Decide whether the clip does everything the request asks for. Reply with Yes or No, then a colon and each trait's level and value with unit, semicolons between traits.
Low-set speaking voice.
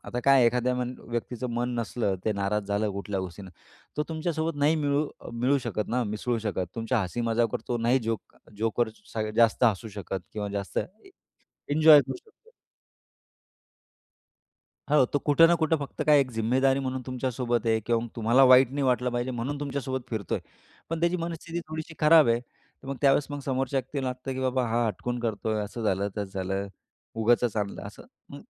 Yes: low, 125 Hz